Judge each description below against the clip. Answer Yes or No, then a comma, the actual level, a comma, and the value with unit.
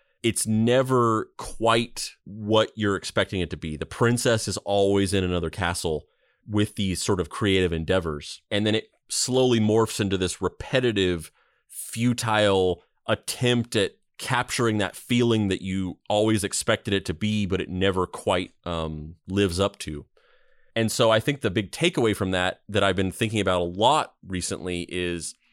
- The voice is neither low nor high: No, low, 100 Hz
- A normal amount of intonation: Yes, average, 3.3 semitones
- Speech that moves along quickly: No, average, 160 wpm